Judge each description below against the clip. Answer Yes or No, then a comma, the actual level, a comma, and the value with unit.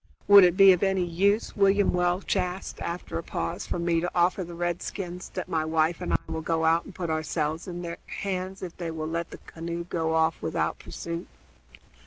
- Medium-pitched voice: Yes, medium, 175 Hz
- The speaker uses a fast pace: Yes, fast, 210 wpm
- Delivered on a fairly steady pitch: Yes, narrow, 1.9 semitones